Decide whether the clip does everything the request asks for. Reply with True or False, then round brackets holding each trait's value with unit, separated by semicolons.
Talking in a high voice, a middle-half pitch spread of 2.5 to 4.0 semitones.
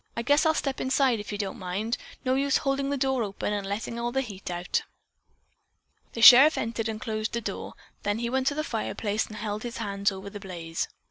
False (225 Hz; 4.5 semitones)